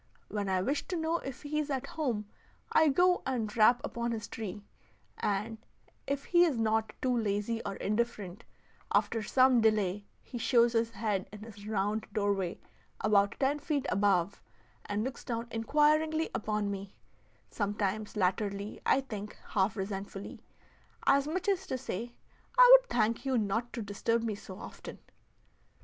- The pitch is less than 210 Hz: No, high, 225 Hz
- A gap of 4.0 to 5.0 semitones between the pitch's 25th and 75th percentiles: Yes, average, 4.5 semitones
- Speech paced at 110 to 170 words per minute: Yes, average, 160 wpm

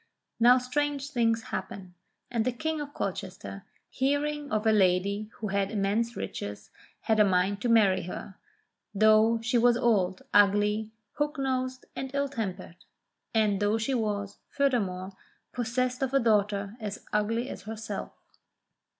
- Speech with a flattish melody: No, average, 3.9 semitones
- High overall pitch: Yes, high, 220 Hz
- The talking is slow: No, average, 145 wpm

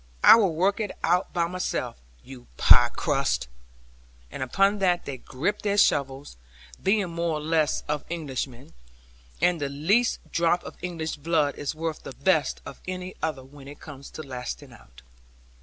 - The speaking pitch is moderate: Yes, medium, 160 Hz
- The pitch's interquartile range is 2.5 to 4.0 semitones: No, average, 4.6 semitones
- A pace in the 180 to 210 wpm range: No, average, 165 wpm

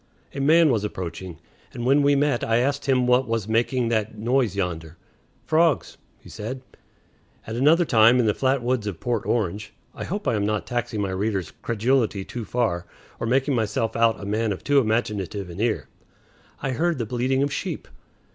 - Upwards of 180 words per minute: Yes, average, 190 wpm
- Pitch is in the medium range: No, low, 115 Hz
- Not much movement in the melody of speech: No, average, 4.0 semitones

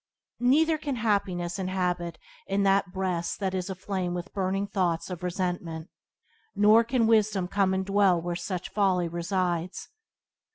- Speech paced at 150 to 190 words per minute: No, average, 140 wpm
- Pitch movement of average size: No, narrow, 2.3 semitones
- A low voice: No, high, 190 Hz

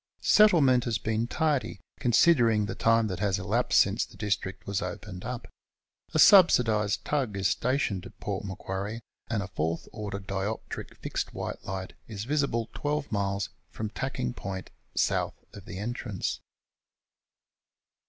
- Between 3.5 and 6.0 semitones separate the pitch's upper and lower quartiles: Yes, average, 4.0 semitones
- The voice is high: No, low, 105 Hz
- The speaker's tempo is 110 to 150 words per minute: Yes, average, 145 wpm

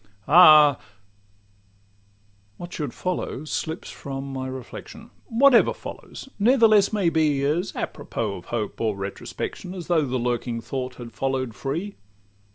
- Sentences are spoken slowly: Yes, slow, 130 wpm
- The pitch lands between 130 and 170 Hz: Yes, low, 135 Hz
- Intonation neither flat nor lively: No, wide, 8.9 semitones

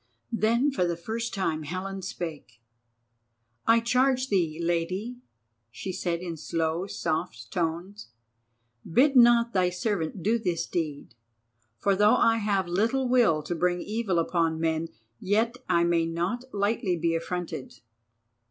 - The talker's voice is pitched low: No, medium, 185 Hz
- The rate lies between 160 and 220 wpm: No, slow, 135 wpm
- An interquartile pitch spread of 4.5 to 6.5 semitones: Yes, average, 5.1 semitones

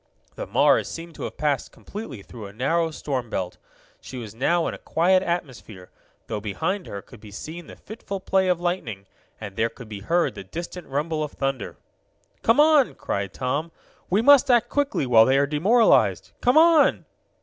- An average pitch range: No, wide, 8.5 semitones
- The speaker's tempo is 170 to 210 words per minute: Yes, average, 185 wpm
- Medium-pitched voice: Yes, medium, 155 Hz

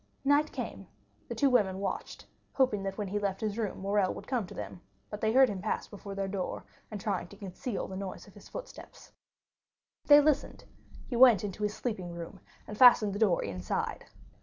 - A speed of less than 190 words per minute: No, fast, 205 wpm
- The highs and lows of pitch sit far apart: No, average, 3.3 semitones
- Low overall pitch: No, high, 205 Hz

